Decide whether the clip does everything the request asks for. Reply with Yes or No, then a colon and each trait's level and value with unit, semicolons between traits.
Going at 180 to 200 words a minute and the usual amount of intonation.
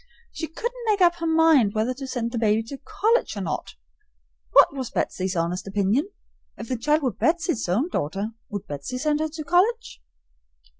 No: average, 185 wpm; wide, 7.7 semitones